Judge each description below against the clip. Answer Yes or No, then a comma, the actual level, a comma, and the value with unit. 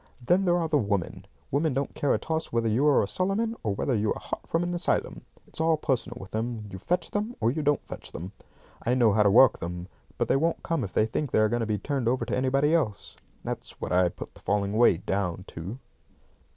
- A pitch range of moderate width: No, wide, 6.9 semitones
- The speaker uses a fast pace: Yes, fast, 245 wpm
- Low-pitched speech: Yes, low, 120 Hz